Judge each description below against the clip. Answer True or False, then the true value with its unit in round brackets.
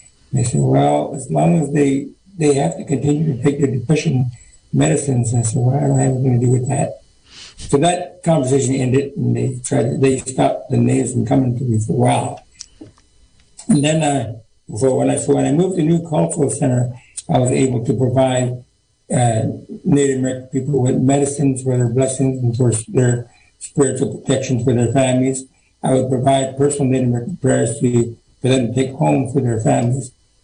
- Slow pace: False (195 wpm)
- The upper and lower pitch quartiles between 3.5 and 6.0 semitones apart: False (2.5 semitones)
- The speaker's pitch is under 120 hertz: False (130 Hz)